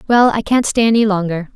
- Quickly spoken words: Yes, fast, 230 wpm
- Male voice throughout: No, female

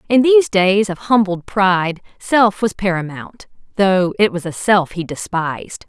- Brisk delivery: No, average, 165 wpm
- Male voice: No, female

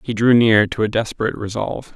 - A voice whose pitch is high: No, low, 110 Hz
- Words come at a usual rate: No, fast, 215 wpm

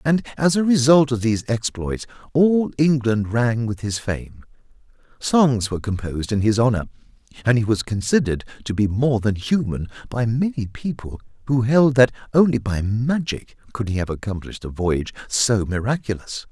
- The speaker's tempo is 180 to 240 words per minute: No, average, 165 wpm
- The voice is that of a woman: No, male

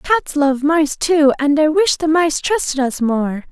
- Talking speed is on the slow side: No, fast, 205 wpm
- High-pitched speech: Yes, very high, 300 Hz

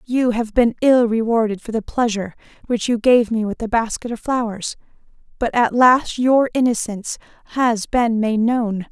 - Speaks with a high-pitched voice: Yes, high, 230 Hz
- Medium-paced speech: Yes, average, 175 wpm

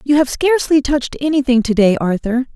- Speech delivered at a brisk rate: No, average, 190 wpm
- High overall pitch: Yes, very high, 265 Hz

